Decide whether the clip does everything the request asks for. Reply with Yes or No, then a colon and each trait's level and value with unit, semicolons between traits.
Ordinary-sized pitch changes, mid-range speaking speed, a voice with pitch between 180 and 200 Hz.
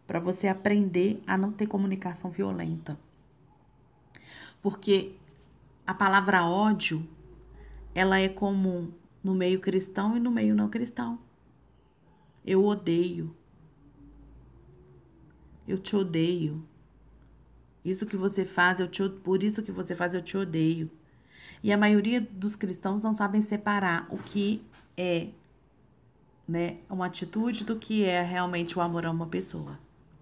Yes: average, 3.6 semitones; average, 130 wpm; medium, 185 Hz